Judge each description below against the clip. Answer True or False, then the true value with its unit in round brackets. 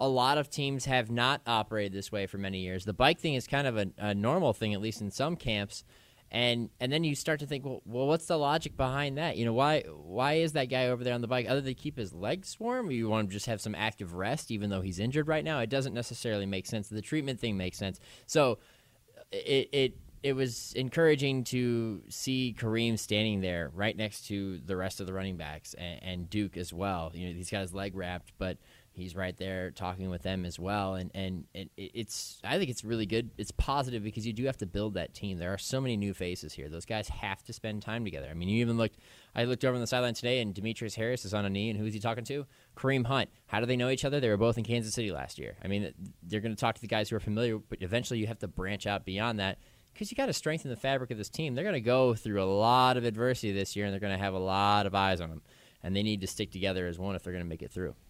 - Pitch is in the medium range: False (110 Hz)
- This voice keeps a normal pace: False (275 wpm)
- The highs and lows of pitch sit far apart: False (4.6 semitones)